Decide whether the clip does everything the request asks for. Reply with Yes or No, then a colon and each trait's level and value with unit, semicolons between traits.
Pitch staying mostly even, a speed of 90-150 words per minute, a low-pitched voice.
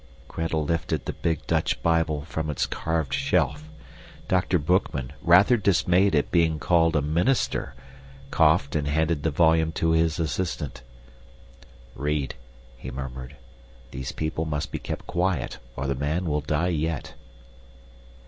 Yes: narrow, 2.3 semitones; average, 140 wpm; very low, 80 Hz